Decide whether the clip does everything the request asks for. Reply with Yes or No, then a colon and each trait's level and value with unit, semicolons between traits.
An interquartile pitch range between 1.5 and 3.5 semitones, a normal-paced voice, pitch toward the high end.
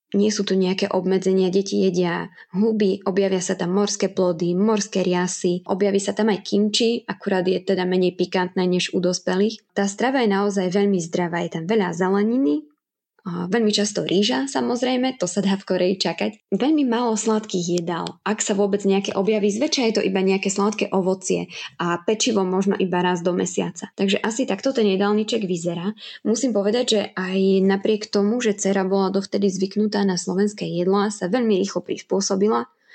No: narrow, 2.5 semitones; fast, 175 wpm; high, 195 Hz